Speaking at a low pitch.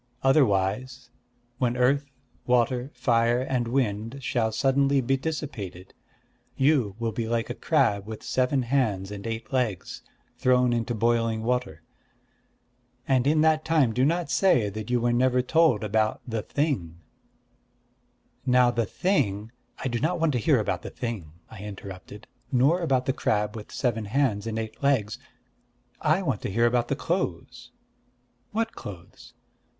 Yes: low, 120 Hz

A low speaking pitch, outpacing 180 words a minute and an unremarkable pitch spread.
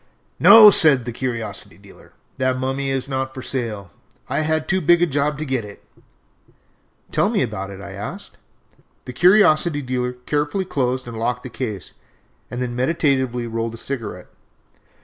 No: low, 130 Hz; average, 165 wpm; average, 3.7 semitones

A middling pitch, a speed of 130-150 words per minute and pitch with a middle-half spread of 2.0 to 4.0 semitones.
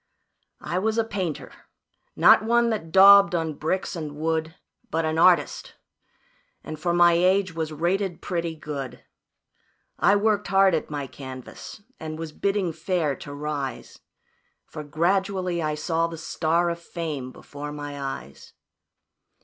Yes: medium, 165 Hz; average, 140 wpm; average, 3.7 semitones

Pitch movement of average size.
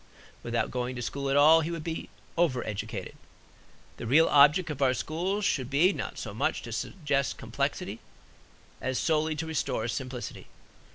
Yes: average, 3.9 semitones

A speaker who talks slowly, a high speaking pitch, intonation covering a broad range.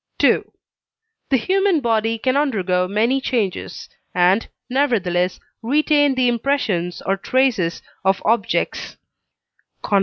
Yes: slow, 100 wpm; high, 230 Hz; wide, 5.9 semitones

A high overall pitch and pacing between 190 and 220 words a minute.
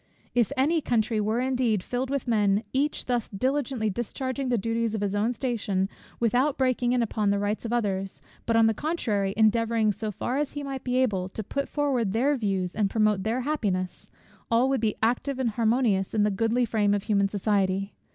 Yes: high, 225 Hz; average, 195 wpm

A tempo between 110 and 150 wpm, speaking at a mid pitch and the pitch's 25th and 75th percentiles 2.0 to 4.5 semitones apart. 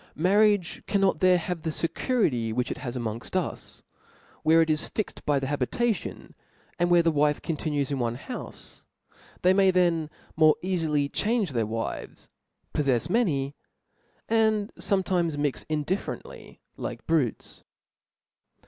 No: average, 140 wpm; medium, 160 Hz; average, 4.9 semitones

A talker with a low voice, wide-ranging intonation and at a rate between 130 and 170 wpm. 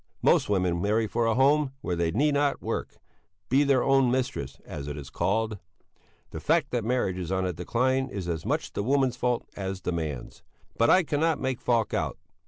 No: low, 115 Hz; wide, 6.6 semitones; average, 200 wpm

